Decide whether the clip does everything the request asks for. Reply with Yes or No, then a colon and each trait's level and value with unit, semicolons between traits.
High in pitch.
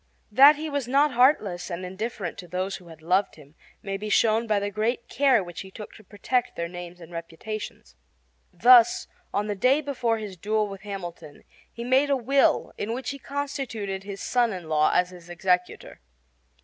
Yes: high, 205 Hz